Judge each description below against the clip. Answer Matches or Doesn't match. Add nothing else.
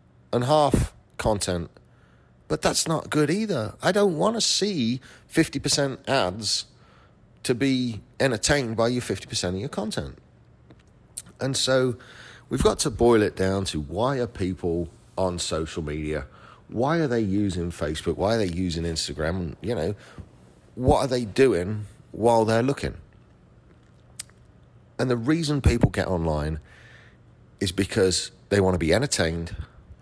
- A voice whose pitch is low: Matches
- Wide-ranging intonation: Matches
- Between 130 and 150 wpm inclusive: Matches